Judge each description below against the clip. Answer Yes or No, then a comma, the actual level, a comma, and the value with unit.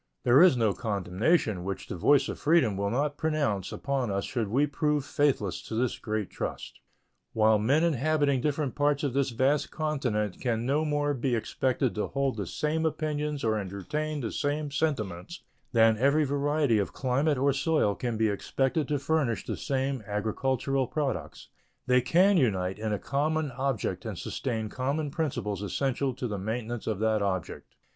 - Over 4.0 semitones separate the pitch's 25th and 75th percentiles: Yes, average, 5.1 semitones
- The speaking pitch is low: Yes, low, 130 Hz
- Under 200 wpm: Yes, average, 170 wpm